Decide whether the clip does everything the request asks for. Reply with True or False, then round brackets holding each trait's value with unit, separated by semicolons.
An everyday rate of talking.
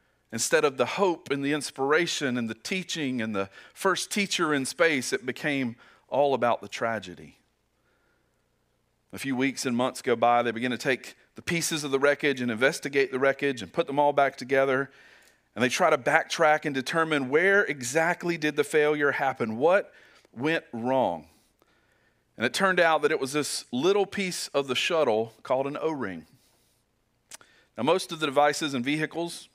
True (180 wpm)